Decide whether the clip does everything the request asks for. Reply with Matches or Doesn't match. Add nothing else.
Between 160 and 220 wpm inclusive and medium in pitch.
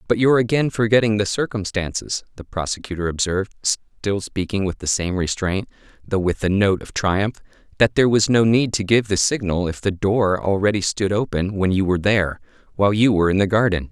Doesn't match